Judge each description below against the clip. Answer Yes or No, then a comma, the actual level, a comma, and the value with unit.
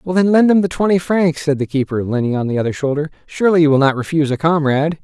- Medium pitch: Yes, medium, 155 Hz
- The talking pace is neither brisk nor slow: No, fast, 260 wpm